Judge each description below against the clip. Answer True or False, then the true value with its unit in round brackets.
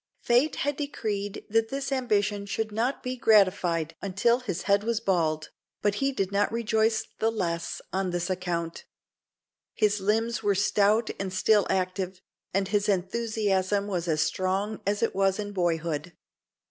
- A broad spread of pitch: False (3.1 semitones)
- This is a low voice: False (200 Hz)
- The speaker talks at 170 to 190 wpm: False (155 wpm)